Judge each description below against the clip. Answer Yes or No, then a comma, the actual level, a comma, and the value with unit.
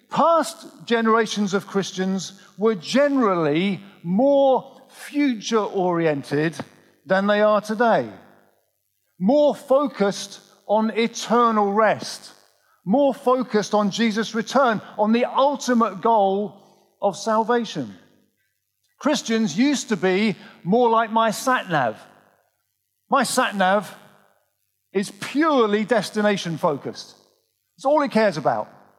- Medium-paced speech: No, slow, 100 wpm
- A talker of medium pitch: No, high, 220 Hz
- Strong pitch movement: No, average, 4.0 semitones